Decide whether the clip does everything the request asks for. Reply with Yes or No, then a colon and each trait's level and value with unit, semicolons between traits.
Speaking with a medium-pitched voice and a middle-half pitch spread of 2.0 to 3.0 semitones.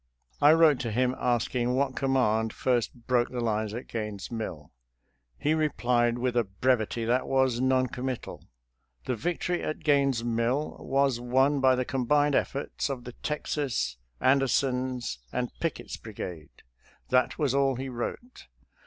No: low, 125 Hz; narrow, 2.6 semitones